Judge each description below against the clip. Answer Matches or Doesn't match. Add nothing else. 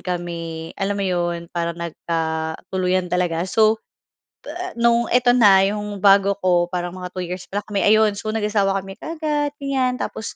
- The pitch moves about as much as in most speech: Matches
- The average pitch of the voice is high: Matches